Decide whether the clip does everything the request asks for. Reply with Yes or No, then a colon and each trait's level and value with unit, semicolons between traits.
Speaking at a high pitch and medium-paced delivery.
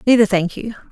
Yes: high, 210 Hz; average, 195 wpm